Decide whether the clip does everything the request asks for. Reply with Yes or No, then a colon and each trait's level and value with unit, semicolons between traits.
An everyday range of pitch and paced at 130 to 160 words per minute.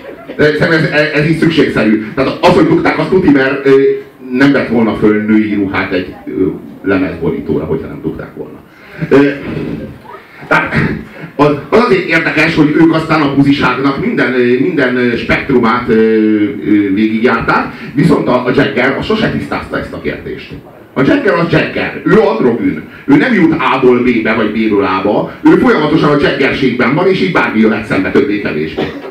Yes: average, 4.6 semitones; average, 150 wpm